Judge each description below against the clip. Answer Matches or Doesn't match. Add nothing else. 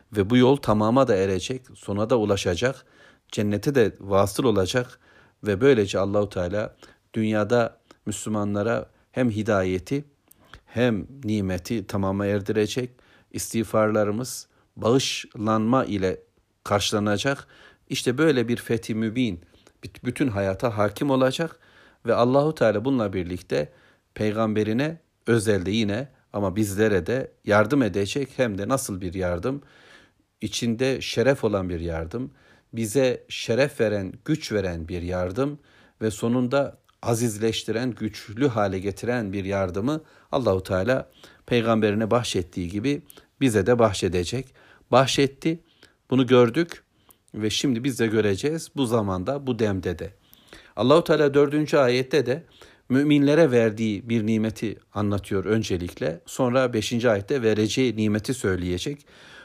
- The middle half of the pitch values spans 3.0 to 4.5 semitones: Matches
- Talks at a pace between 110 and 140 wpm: Matches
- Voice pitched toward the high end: Doesn't match